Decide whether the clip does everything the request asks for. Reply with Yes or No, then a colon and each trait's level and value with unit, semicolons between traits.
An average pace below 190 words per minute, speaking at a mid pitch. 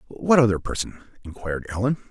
No: average, 140 wpm; low, 110 Hz